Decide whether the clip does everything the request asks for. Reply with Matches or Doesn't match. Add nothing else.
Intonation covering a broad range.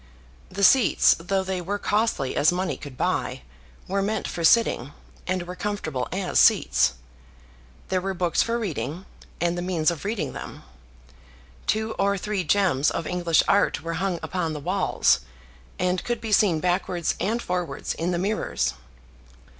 Doesn't match